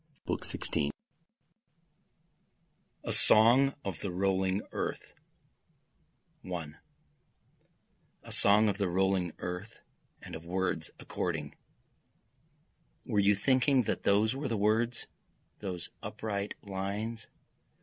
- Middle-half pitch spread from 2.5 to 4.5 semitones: Yes, average, 3.3 semitones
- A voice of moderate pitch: No, low, 100 Hz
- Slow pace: Yes, slow, 100 wpm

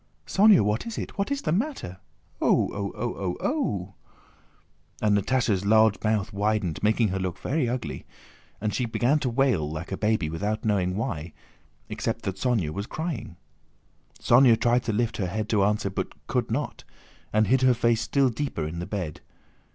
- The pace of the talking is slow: No, average, 175 wpm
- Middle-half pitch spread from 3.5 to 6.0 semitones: Yes, average, 4.3 semitones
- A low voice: Yes, low, 110 Hz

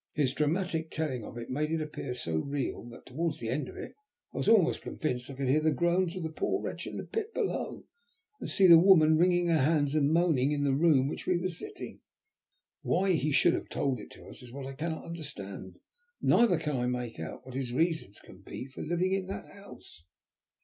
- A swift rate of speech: Yes, fast, 230 wpm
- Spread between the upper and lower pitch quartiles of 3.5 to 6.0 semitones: Yes, average, 4.6 semitones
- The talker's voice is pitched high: No, medium, 155 Hz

